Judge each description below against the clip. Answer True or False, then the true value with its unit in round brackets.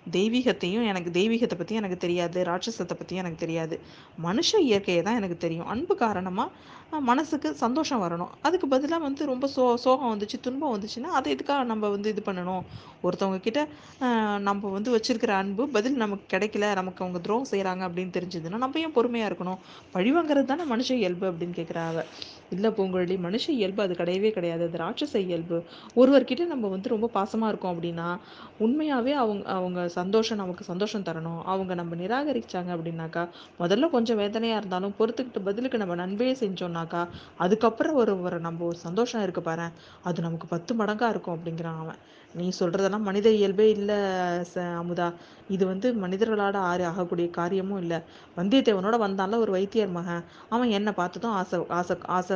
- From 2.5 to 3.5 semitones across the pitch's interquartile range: False (4.7 semitones)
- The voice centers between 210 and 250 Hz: False (195 Hz)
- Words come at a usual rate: False (155 wpm)